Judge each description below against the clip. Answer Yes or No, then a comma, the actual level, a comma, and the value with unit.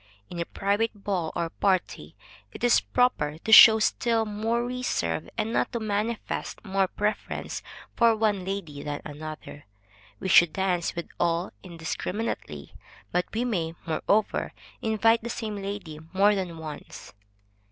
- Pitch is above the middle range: Yes, high, 195 Hz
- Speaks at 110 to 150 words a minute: Yes, average, 140 wpm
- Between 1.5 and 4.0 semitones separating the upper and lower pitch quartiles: No, average, 4.8 semitones